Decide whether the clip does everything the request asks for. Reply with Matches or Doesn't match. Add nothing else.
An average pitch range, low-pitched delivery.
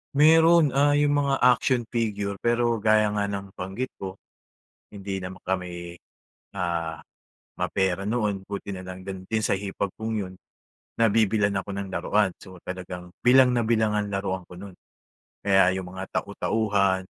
Matches